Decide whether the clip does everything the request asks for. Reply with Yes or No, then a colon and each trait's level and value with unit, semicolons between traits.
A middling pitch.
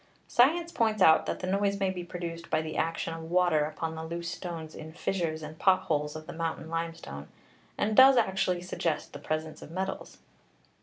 Yes: medium, 170 Hz